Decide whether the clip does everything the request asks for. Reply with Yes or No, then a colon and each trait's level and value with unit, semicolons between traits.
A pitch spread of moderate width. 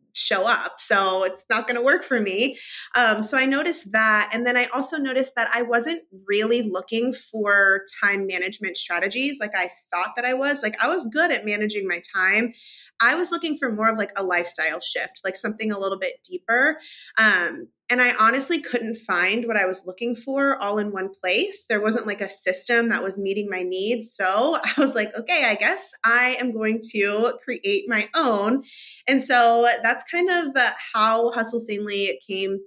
Yes: average, 4.2 semitones